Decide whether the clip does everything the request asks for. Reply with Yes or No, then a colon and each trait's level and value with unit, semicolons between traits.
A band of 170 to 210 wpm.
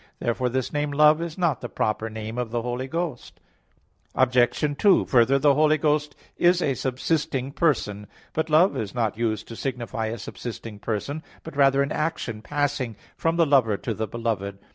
Yes: average, 180 wpm